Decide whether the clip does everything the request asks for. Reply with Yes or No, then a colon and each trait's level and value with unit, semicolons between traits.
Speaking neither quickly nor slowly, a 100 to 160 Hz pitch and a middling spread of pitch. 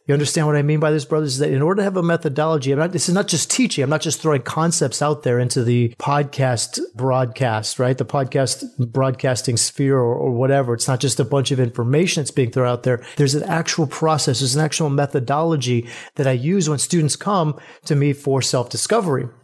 No: fast, 225 wpm; medium, 140 Hz; average, 3.3 semitones